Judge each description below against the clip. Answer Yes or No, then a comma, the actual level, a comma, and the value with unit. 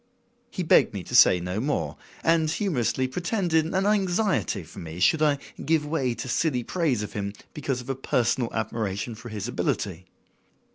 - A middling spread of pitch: No, wide, 7.0 semitones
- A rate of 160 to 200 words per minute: Yes, average, 175 wpm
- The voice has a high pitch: No, low, 130 Hz